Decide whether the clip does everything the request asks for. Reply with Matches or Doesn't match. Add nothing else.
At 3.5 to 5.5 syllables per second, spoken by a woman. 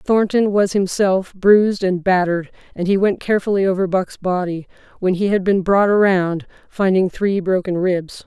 Matches